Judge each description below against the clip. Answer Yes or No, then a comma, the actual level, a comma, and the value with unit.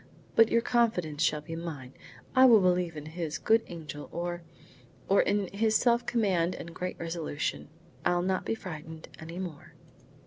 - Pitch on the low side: No, medium, 175 Hz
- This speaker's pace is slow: No, average, 165 wpm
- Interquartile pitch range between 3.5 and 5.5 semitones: Yes, average, 4.2 semitones